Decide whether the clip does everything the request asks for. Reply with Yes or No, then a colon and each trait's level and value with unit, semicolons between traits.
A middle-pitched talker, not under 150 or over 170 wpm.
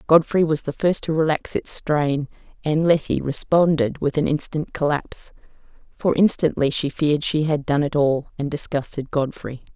Yes: medium, 150 Hz; average, 165 wpm